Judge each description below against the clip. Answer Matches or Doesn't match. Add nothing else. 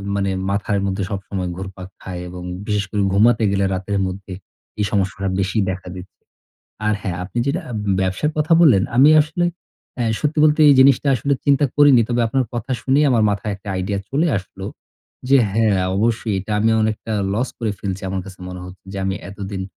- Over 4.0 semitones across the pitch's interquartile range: Matches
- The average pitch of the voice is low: Matches